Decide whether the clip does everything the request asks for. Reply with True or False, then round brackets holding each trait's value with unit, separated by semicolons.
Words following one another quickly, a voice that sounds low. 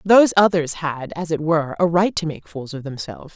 False (235 wpm; 165 Hz)